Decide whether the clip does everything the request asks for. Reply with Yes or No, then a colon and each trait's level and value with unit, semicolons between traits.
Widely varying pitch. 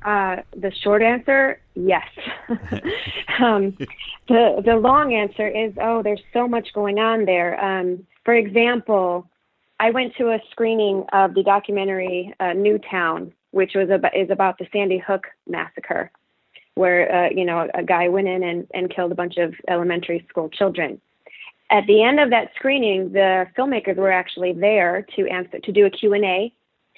No: average, 3.3 semitones